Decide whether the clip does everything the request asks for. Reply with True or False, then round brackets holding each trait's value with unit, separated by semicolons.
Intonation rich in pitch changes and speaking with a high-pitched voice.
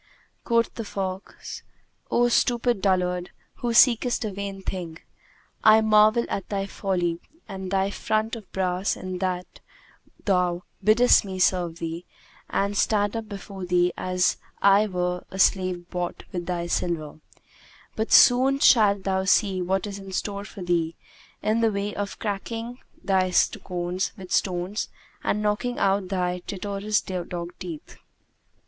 False (2.8 semitones; 195 Hz)